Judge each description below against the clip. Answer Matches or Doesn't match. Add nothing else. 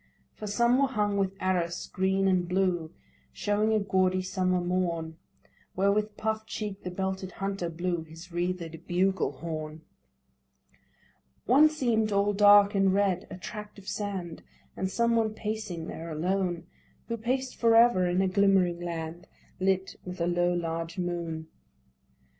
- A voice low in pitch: Doesn't match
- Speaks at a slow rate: Doesn't match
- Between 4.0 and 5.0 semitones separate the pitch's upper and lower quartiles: Doesn't match